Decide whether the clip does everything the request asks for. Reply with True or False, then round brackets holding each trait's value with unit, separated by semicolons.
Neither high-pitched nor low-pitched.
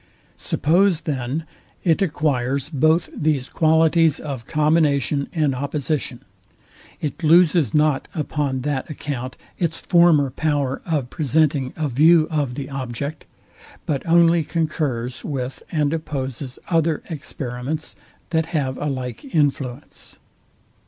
True (150 Hz)